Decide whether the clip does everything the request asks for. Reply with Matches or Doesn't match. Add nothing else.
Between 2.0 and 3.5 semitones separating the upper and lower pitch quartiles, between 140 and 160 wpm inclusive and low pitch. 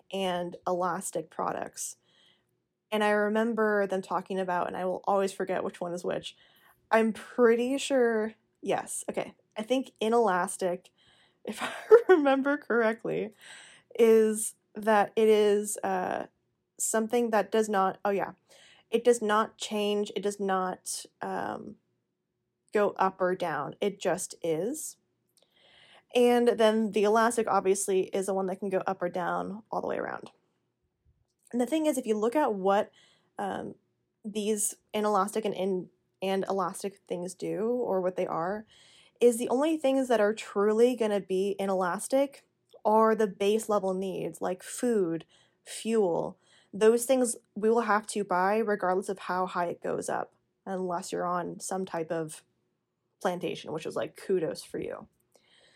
Doesn't match